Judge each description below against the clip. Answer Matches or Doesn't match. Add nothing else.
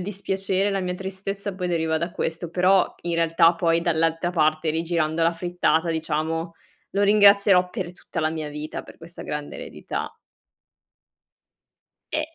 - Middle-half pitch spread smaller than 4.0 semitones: Matches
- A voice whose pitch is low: Doesn't match